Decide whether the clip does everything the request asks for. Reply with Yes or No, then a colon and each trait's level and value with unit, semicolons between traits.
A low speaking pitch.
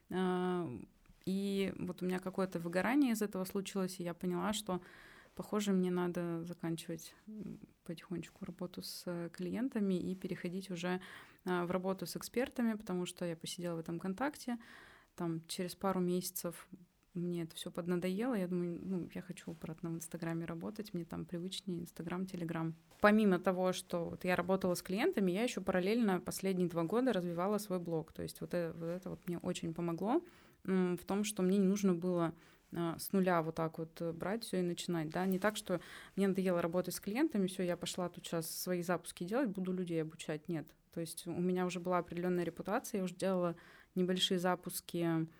No: medium, 180 Hz